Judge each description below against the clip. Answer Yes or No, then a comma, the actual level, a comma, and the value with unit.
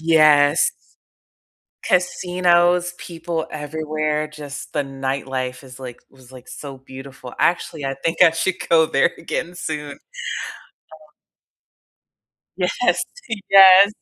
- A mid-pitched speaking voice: Yes, medium, 155 Hz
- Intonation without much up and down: No, average, 4.1 semitones